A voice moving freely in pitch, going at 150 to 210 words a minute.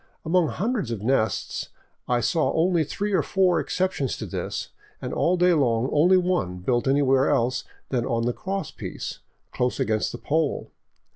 Yes: wide, 6.8 semitones; average, 170 wpm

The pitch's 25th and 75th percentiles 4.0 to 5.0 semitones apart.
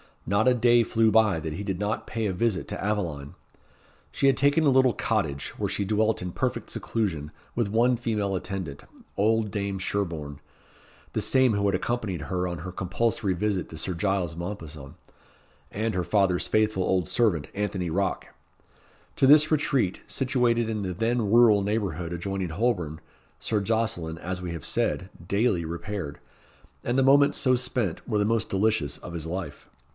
Yes: average, 4.4 semitones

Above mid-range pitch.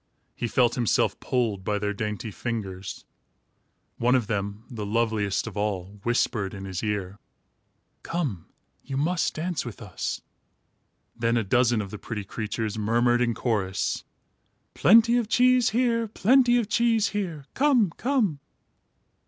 No: low, 115 Hz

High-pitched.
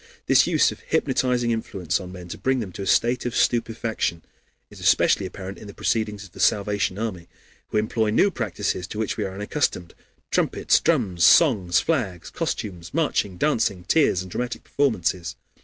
No: low, 105 Hz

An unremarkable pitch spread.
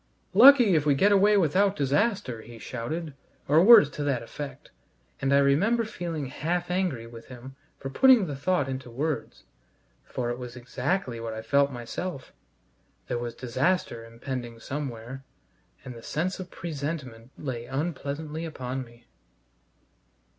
No: wide, 6.1 semitones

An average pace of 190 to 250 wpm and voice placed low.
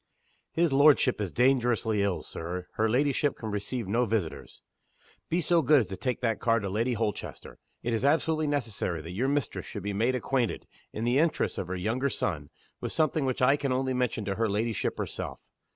Yes: average, 200 wpm; low, 120 Hz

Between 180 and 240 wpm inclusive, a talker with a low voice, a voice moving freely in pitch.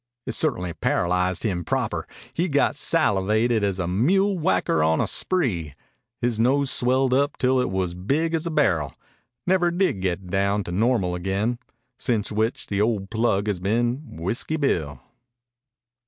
No: average, 155 wpm; low, 110 Hz; wide, 6.7 semitones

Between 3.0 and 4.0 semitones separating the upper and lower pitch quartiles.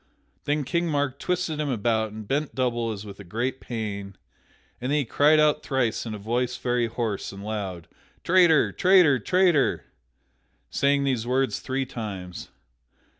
No: average, 5.0 semitones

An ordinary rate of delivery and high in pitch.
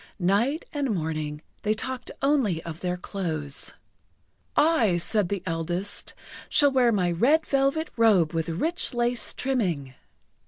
No: slow, 130 wpm; high, 205 Hz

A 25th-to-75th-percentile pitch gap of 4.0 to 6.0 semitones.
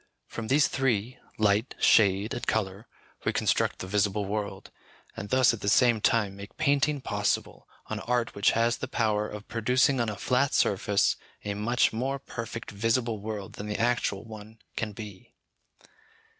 No: average, 3.0 semitones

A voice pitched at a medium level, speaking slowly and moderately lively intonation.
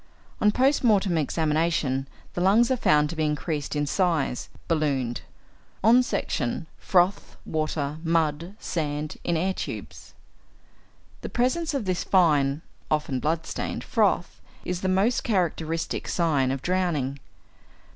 Yes: medium, 165 Hz; slow, 130 wpm; average, 4.1 semitones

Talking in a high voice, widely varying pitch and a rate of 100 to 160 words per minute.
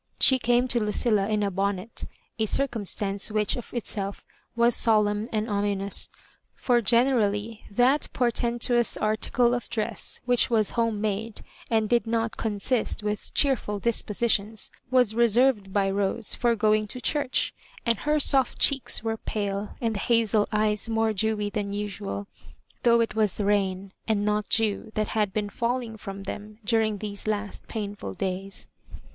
No: high, 215 Hz; narrow, 2.4 semitones; average, 155 wpm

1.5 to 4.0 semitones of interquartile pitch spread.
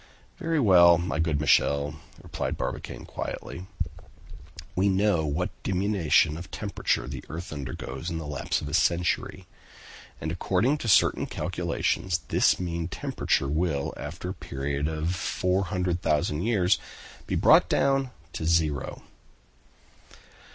Yes: average, 3.5 semitones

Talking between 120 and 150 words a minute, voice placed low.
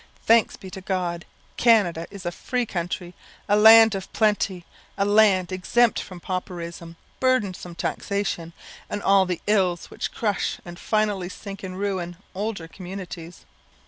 No: average, 145 wpm; high, 190 Hz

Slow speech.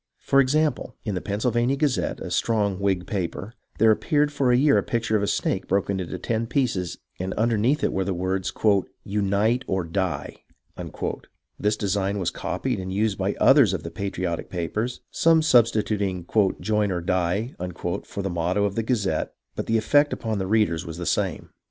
No: average, 180 wpm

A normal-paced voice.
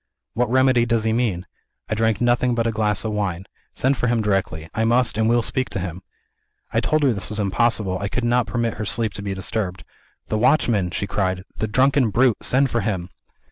No: fast, 220 wpm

